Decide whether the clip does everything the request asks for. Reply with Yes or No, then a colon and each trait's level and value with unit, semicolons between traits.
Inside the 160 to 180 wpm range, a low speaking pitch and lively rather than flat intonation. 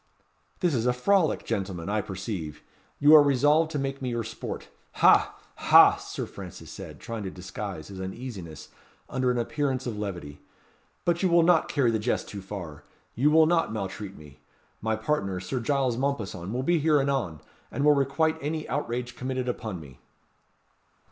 Yes: average, 175 wpm; low, 120 Hz; wide, 6.7 semitones